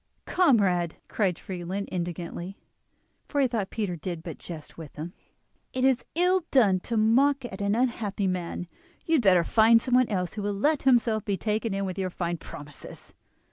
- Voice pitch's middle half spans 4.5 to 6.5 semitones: Yes, average, 5.2 semitones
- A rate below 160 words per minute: No, average, 180 wpm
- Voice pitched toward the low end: No, high, 200 Hz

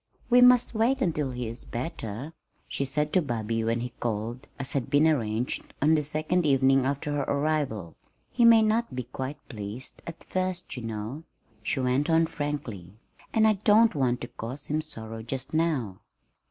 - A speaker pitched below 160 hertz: Yes, medium, 140 Hz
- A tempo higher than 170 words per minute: Yes, average, 180 wpm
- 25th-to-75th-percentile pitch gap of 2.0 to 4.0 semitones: No, average, 5.3 semitones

